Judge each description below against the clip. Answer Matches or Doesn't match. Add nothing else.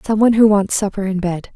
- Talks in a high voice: Matches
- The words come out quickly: Matches